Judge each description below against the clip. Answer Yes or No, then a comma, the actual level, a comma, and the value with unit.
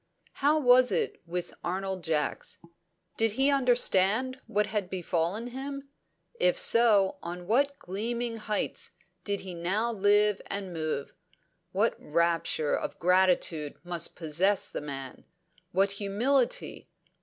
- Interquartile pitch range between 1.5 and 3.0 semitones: No, average, 5.2 semitones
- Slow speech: Yes, slow, 120 wpm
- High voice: Yes, high, 200 Hz